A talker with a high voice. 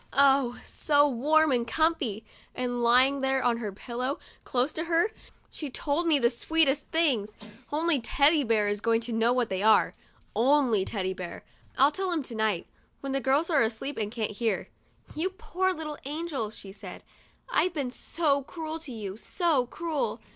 Yes: very high, 265 Hz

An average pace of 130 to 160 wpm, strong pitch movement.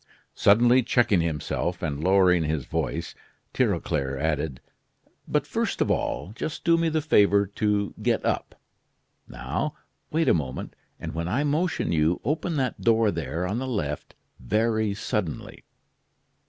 Yes: average, 140 wpm; wide, 7.2 semitones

